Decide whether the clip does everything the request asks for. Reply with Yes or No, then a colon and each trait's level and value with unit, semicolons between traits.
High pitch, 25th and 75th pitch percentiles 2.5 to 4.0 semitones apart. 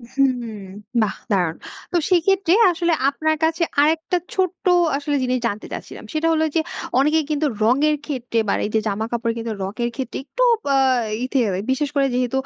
No: very high, 280 Hz; average, 5.1 semitones